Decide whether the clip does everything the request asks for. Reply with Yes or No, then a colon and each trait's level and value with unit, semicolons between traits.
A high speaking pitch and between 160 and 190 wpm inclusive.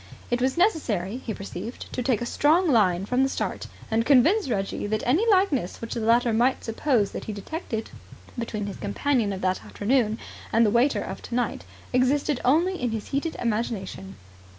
Yes: high, 240 Hz; average, 180 wpm